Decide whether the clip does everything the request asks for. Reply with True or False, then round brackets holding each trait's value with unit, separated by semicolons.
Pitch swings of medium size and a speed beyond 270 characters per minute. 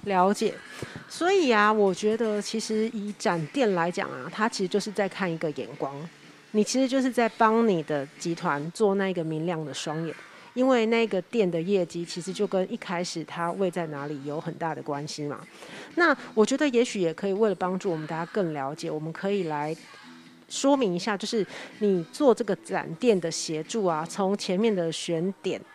True (4.8 semitones; 280 characters per minute)